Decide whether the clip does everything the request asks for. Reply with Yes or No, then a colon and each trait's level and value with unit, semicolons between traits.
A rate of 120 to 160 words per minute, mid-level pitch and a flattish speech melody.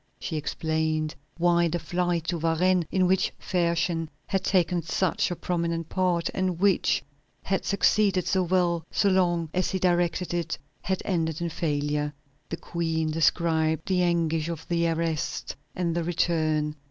Yes: average, 155 wpm; medium, 170 Hz; narrow, 1.9 semitones